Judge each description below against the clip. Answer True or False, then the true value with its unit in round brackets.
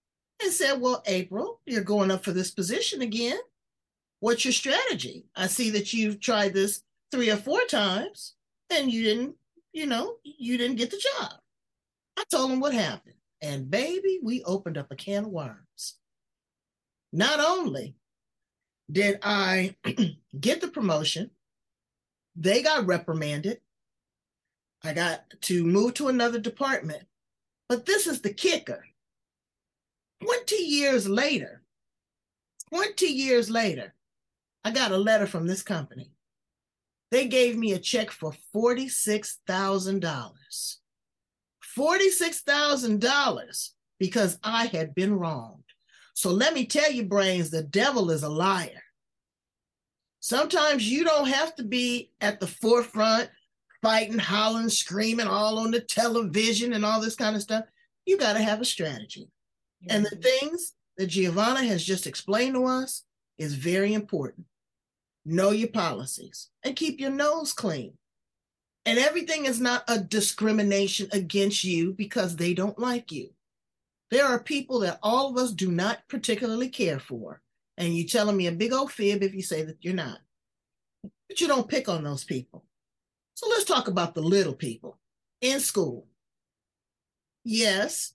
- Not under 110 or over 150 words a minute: True (145 wpm)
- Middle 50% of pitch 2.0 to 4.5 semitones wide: False (5.4 semitones)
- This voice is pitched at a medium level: False (220 Hz)